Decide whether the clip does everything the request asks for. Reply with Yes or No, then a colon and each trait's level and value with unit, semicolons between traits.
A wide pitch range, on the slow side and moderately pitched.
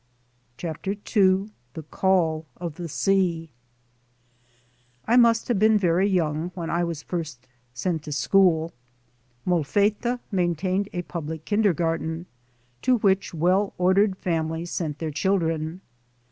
No: average, 3.3 semitones; slow, 120 wpm; medium, 175 Hz